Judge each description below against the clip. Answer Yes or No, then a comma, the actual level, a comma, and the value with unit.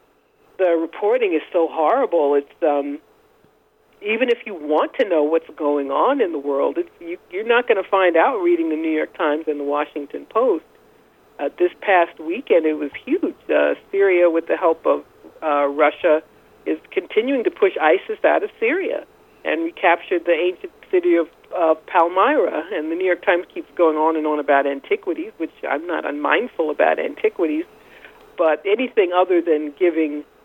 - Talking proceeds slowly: No, average, 180 wpm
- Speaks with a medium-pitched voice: Yes, medium, 180 Hz